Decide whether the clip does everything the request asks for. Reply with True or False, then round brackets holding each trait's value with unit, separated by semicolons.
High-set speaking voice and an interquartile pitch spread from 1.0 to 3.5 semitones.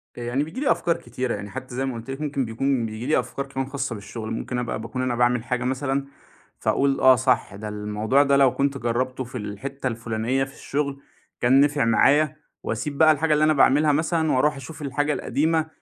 False (130 Hz; 3.0 semitones)